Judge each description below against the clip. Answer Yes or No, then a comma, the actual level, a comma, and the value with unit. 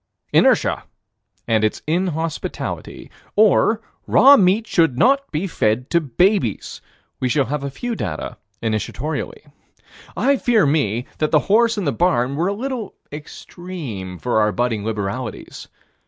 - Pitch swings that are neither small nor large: No, wide, 9.0 semitones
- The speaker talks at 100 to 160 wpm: Yes, average, 140 wpm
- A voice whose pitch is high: No, medium, 155 Hz